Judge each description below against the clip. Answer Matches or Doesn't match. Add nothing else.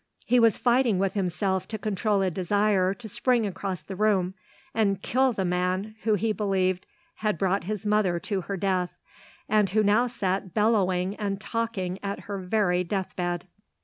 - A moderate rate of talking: Matches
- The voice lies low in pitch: Doesn't match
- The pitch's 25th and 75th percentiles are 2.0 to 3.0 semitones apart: Matches